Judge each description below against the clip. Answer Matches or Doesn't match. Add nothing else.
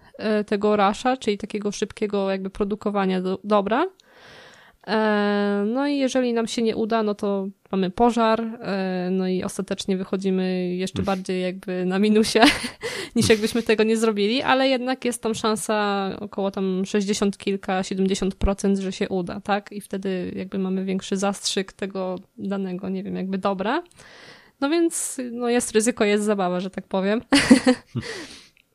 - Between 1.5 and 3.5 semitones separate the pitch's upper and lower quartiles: Matches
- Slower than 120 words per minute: Doesn't match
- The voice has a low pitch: Doesn't match